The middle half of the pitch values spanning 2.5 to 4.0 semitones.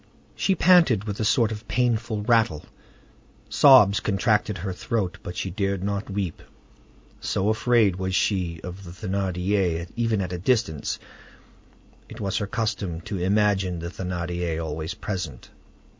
Yes: average, 3.4 semitones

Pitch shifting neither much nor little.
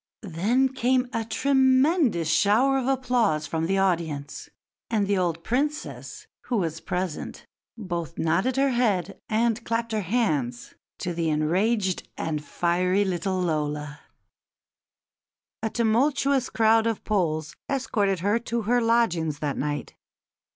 No: wide, 6.2 semitones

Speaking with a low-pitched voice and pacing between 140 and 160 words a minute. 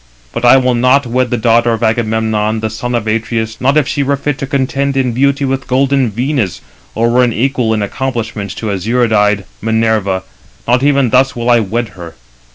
No: low, 120 Hz; average, 195 wpm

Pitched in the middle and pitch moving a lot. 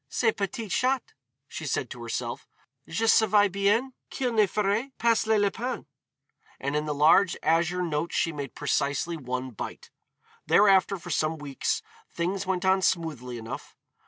Yes: medium, 180 Hz; wide, 6.0 semitones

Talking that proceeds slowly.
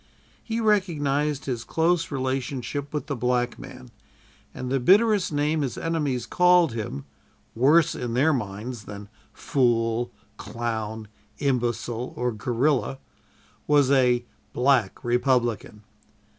Yes: slow, 115 wpm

